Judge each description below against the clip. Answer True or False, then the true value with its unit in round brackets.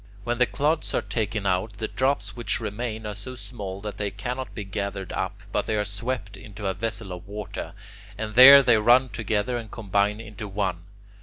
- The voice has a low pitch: True (105 Hz)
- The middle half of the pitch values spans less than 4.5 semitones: True (3.0 semitones)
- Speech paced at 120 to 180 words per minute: False (200 wpm)